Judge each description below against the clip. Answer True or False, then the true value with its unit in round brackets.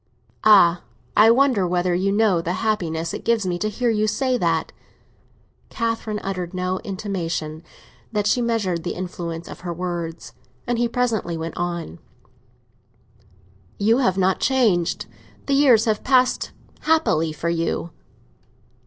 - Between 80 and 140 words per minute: True (135 wpm)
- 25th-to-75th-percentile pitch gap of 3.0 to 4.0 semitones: False (4.9 semitones)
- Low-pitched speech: False (190 Hz)